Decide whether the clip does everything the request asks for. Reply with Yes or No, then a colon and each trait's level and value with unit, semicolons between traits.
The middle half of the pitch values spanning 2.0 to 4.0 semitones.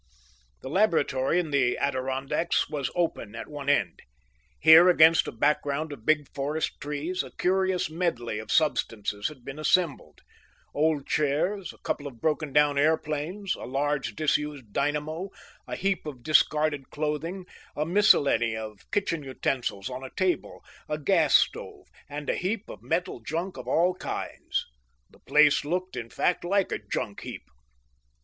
Yes: average, 3.7 semitones